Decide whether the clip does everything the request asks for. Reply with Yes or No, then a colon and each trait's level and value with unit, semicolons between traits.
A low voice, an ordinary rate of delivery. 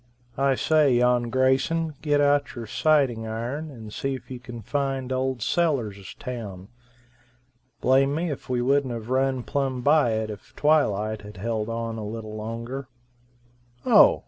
Yes: low, 125 Hz; average, 155 wpm